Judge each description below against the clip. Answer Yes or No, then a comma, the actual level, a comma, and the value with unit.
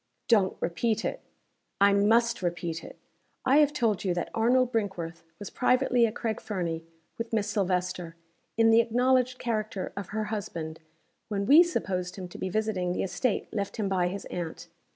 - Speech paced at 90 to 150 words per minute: No, average, 175 wpm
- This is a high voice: Yes, high, 205 Hz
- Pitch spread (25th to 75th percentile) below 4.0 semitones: No, average, 4.3 semitones